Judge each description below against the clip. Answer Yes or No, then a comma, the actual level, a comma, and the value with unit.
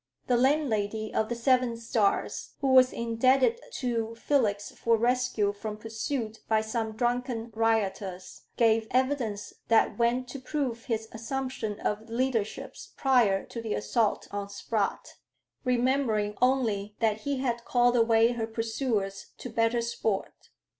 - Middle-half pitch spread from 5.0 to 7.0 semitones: No, narrow, 2.6 semitones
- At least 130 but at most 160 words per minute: Yes, slow, 135 wpm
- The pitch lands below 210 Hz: No, high, 230 Hz